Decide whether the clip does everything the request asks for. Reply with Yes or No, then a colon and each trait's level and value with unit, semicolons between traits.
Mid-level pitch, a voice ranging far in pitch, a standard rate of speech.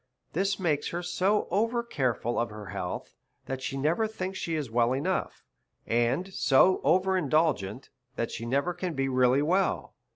Yes: medium, 150 Hz; wide, 6.6 semitones; average, 165 wpm